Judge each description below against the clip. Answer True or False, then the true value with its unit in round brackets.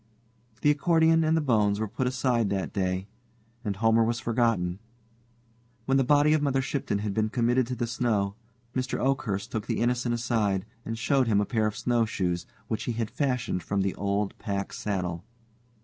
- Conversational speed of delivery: True (180 wpm)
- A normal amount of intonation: True (4.1 semitones)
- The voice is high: False (115 Hz)